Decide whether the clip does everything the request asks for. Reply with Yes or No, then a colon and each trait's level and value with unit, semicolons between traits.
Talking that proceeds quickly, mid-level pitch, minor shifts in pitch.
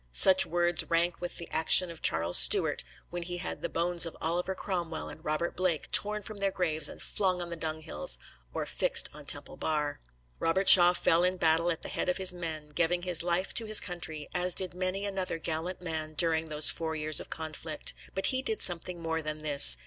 Yes: fast, 210 wpm; medium, 170 Hz; narrow, 2.3 semitones